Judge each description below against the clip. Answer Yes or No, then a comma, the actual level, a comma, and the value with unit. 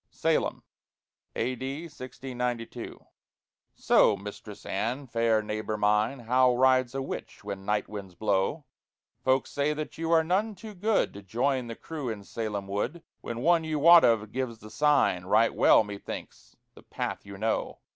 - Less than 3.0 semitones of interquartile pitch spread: No, average, 5.2 semitones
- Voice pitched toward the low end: Yes, low, 120 Hz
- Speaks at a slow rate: No, average, 155 wpm